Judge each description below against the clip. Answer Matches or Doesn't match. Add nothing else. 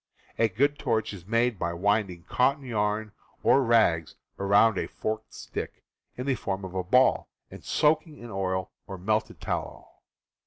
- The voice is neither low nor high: Doesn't match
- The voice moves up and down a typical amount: Matches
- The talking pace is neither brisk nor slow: Matches